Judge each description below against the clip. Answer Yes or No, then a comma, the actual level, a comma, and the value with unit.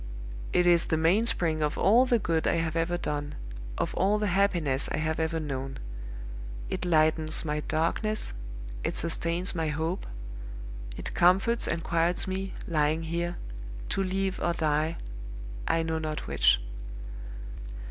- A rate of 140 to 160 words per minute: Yes, average, 145 wpm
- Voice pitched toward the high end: No, medium, 165 Hz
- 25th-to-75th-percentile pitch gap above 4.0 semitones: No, average, 2.7 semitones